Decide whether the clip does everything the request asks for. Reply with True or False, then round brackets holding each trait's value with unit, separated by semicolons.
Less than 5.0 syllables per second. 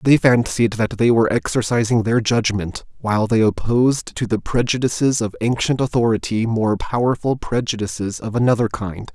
False (5.2 syllables/s)